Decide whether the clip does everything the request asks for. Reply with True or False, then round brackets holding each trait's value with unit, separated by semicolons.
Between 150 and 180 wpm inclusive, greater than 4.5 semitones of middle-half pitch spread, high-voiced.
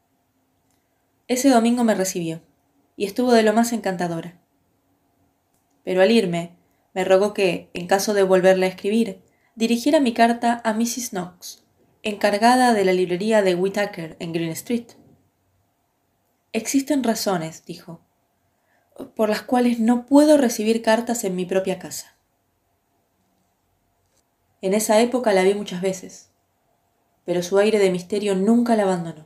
False (135 wpm; 5.1 semitones; 195 Hz)